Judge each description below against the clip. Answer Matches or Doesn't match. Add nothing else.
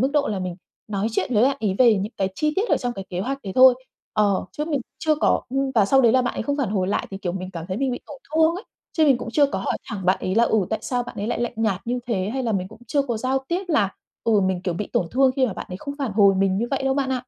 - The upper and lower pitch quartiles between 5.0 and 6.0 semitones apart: Matches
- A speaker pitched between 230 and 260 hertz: Matches